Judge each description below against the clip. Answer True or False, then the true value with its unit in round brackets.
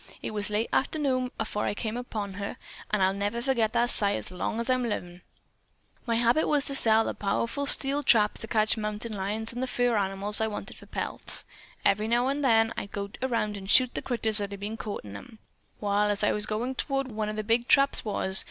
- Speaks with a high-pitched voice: True (220 Hz)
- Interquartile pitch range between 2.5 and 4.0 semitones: True (2.9 semitones)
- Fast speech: True (235 wpm)